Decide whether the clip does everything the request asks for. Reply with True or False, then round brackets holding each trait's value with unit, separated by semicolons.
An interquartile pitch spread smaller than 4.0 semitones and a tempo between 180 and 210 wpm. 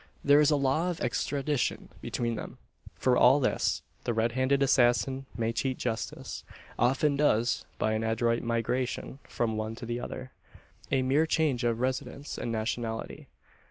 False (3.0 semitones; 160 wpm)